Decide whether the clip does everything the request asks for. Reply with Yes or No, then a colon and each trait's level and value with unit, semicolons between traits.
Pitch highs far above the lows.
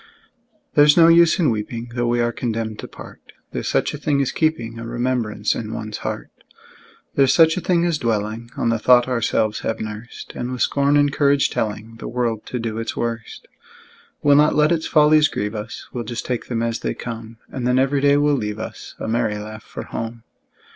No: average, 4.1 semitones